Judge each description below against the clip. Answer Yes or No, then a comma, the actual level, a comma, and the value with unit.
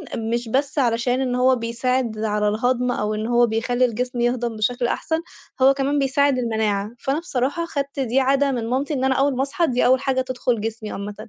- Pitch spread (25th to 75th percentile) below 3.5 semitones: Yes, average, 2.8 semitones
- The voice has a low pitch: No, very high, 250 Hz